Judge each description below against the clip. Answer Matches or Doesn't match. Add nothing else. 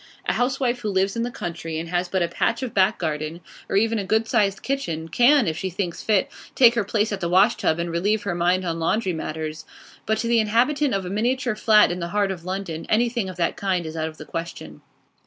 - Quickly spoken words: Matches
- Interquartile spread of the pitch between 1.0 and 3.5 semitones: Doesn't match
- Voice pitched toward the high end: Matches